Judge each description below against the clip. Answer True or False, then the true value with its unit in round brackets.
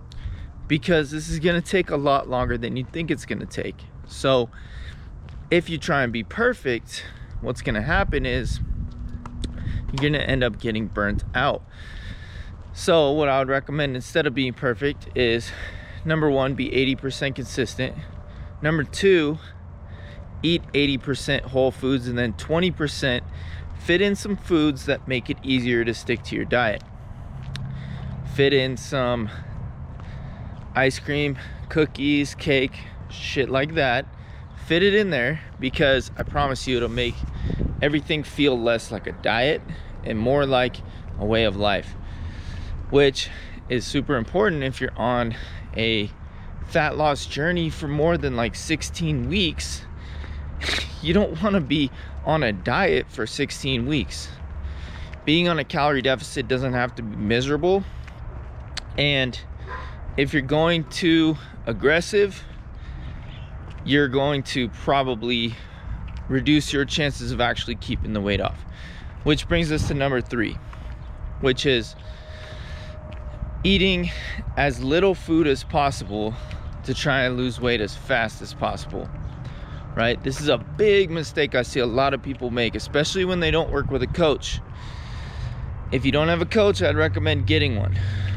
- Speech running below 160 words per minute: True (145 wpm)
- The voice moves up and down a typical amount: False (7.1 semitones)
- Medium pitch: False (125 Hz)